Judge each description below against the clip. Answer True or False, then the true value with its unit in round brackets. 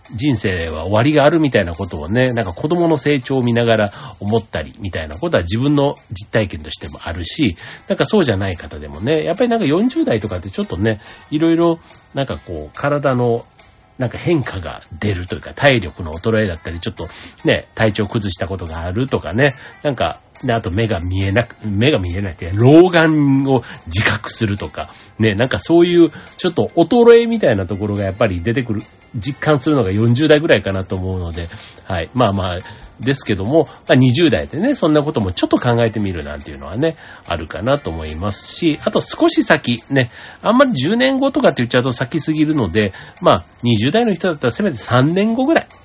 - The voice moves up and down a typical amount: False (7.4 semitones)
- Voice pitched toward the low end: True (115 Hz)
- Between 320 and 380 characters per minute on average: False (395 characters per minute)